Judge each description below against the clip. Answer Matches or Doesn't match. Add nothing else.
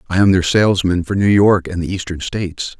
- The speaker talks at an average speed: Doesn't match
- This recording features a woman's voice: Doesn't match